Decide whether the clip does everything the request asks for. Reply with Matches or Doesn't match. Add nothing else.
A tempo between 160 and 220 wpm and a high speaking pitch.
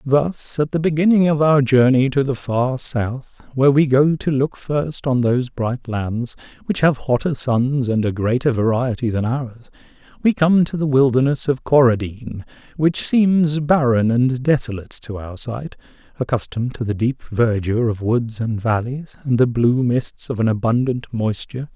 Doesn't match